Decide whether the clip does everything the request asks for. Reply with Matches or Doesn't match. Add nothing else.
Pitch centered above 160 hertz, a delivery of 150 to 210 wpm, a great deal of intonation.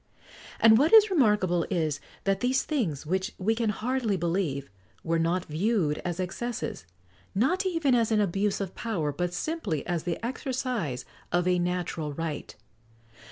Matches